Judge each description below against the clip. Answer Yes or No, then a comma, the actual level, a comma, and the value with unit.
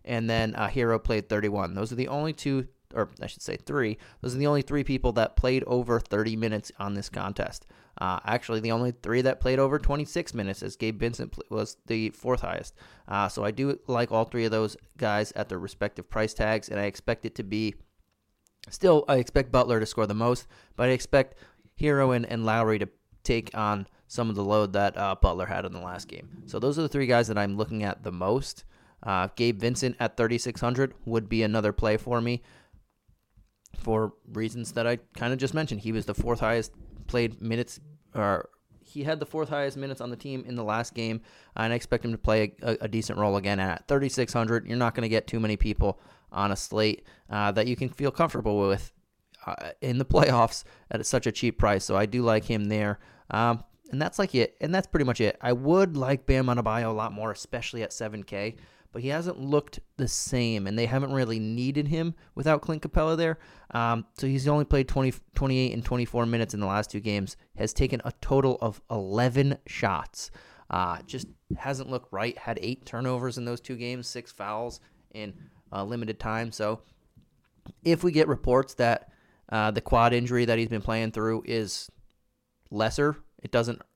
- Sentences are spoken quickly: Yes, fast, 210 wpm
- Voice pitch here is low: Yes, low, 115 Hz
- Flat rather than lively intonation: No, average, 3.3 semitones